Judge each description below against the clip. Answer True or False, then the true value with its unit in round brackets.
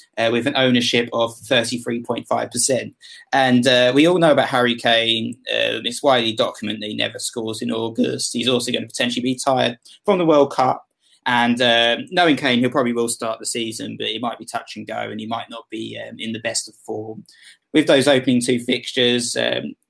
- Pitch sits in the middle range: False (120 Hz)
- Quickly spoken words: True (215 wpm)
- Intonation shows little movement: True (1.7 semitones)